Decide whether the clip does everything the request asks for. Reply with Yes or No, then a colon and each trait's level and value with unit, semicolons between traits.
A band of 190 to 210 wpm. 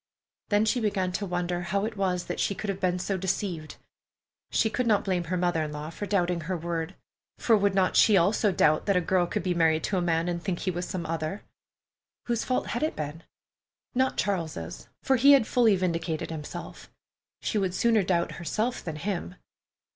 Yes: fast, 205 wpm